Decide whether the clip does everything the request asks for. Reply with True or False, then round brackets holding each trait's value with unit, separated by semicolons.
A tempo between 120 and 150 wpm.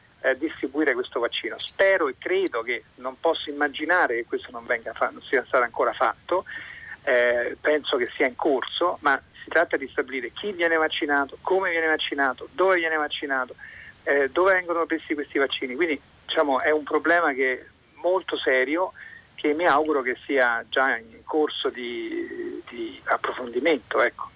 False (165 wpm)